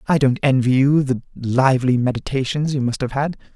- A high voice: No, low, 130 Hz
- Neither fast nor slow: Yes, average, 185 wpm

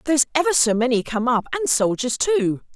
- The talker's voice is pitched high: Yes, very high, 255 Hz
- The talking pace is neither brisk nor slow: Yes, average, 195 wpm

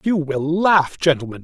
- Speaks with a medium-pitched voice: Yes, medium, 160 Hz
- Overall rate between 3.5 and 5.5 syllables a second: Yes, 4.5 syllables/s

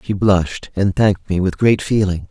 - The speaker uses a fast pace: Yes, fast, 210 wpm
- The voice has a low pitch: Yes, very low, 95 Hz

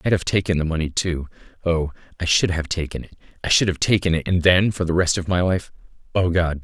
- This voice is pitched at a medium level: No, very low, 85 Hz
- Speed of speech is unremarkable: No, fast, 245 wpm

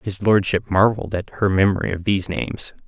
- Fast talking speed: No, average, 190 wpm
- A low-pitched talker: Yes, low, 100 Hz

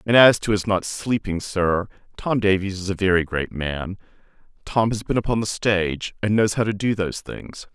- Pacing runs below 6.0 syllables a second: Yes, 5.1 syllables/s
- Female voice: No, male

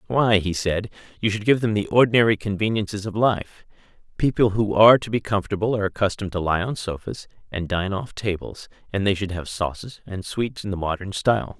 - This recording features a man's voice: Yes, male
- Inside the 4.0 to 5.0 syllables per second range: No, 5.9 syllables/s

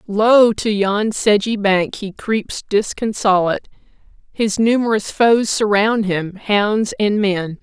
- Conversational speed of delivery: No, slow, 125 wpm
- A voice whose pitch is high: Yes, high, 210 Hz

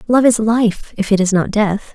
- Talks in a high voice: Yes, high, 215 Hz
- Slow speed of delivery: No, fast, 245 wpm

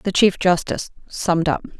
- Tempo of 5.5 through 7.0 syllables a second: No, 5.3 syllables/s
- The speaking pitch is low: No, medium, 170 Hz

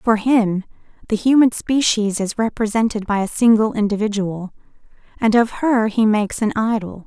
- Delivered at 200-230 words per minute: No, average, 155 wpm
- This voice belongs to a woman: Yes, female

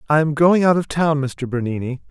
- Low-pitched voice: No, medium, 150 Hz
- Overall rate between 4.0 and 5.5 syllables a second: Yes, 5.4 syllables/s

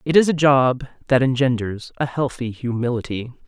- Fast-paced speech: No, average, 155 wpm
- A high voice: No, low, 130 Hz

